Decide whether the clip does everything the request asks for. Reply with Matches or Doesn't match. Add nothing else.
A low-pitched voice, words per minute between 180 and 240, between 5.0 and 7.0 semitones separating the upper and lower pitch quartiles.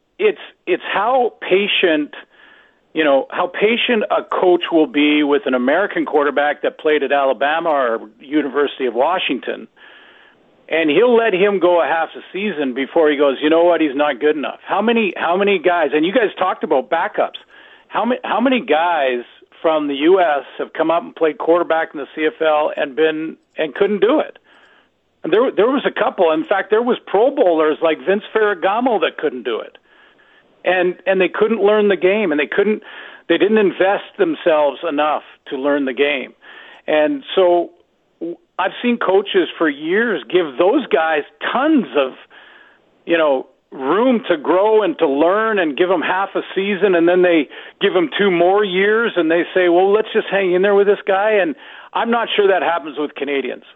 Doesn't match